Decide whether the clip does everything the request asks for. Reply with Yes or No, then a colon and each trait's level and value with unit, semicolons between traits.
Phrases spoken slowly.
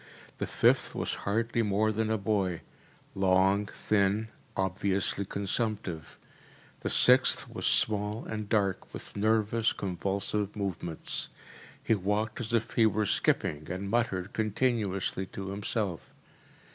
Yes: slow, 120 wpm